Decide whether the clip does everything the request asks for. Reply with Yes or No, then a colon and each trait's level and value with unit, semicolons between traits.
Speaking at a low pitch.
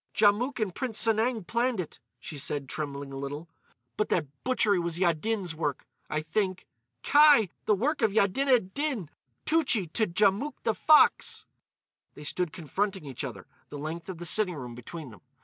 No: high, 190 Hz